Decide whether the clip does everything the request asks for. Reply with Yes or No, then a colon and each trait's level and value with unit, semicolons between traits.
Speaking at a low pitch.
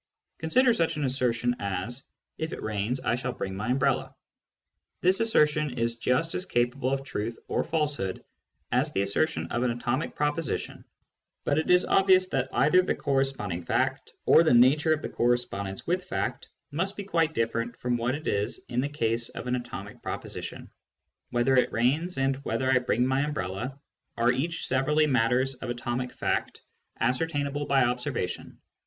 Yes: low, 130 Hz